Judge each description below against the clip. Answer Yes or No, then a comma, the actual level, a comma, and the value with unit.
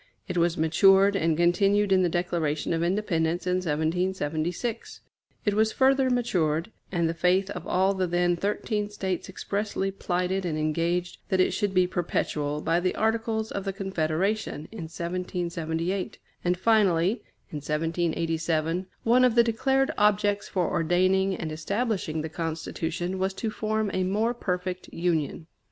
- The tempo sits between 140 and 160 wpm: Yes, average, 150 wpm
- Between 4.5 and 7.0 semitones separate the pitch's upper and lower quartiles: No, average, 3.5 semitones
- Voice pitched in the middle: Yes, medium, 180 Hz